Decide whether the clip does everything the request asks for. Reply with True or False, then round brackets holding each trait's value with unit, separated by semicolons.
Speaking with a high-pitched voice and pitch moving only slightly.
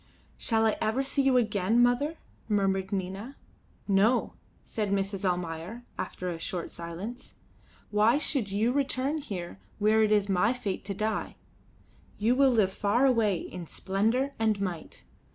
False (210 Hz; 4.0 semitones)